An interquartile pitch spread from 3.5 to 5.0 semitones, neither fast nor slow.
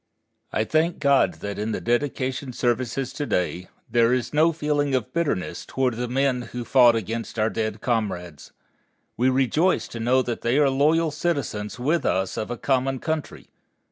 Yes: average, 3.9 semitones; average, 170 wpm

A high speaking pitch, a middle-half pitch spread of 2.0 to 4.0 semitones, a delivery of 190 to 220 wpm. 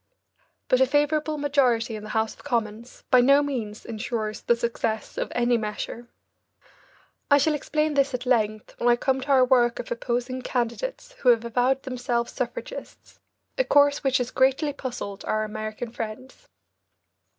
No: high, 245 Hz; average, 3.2 semitones; average, 160 wpm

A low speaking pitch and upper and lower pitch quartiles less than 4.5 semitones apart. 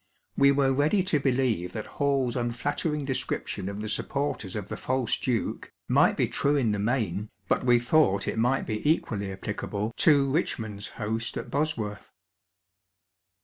No: low, 120 Hz; average, 4.9 semitones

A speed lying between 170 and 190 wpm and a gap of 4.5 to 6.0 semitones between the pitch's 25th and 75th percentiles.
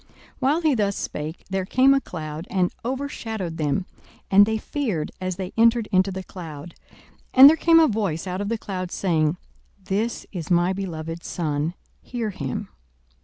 Yes: average, 175 wpm; average, 5.2 semitones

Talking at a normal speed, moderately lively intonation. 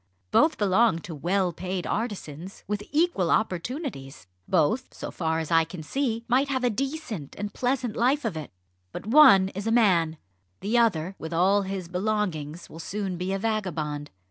No: average, 170 wpm; wide, 5.8 semitones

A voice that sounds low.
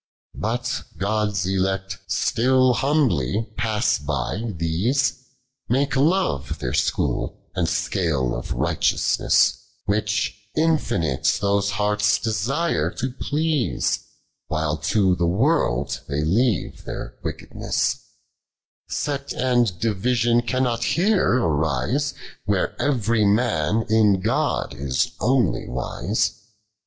Yes: low, 105 Hz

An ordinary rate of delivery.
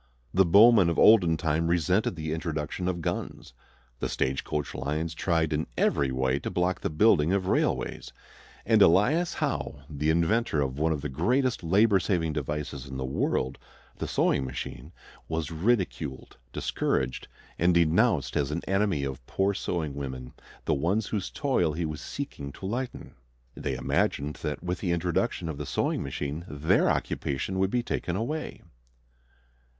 Yes: average, 160 wpm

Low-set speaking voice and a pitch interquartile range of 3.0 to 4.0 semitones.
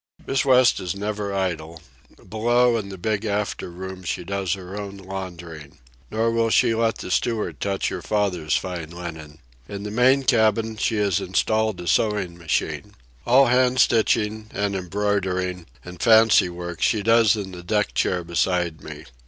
Yes: low, 100 Hz; average, 3.7 semitones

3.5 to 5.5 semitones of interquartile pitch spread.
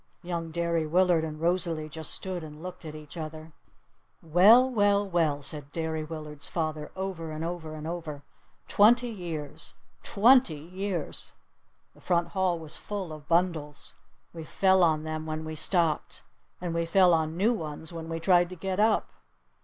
No: average, 2.7 semitones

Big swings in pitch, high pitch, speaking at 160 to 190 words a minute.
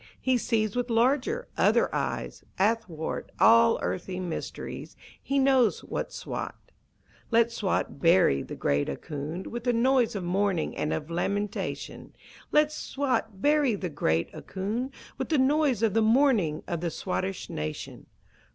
No: wide, 6.3 semitones; high, 220 Hz; average, 140 wpm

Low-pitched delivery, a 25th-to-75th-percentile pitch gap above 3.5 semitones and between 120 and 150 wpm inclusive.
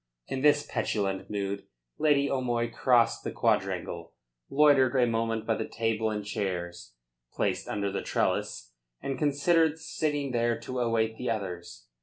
Yes: low, 115 Hz; average, 4.7 semitones; average, 145 wpm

